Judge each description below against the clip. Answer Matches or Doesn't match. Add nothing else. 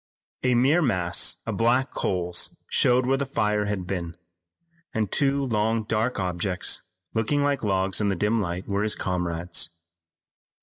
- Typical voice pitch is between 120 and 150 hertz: Doesn't match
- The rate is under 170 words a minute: Matches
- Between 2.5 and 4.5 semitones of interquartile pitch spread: Doesn't match